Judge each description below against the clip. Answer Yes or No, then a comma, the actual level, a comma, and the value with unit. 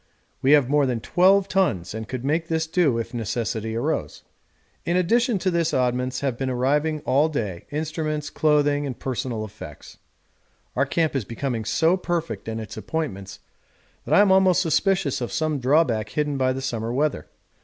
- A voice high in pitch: No, medium, 140 Hz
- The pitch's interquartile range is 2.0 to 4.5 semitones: No, average, 5.3 semitones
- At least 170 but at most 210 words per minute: Yes, average, 175 wpm